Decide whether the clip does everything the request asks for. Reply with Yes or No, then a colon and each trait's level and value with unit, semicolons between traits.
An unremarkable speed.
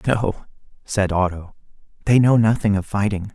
Yes: average, 145 wpm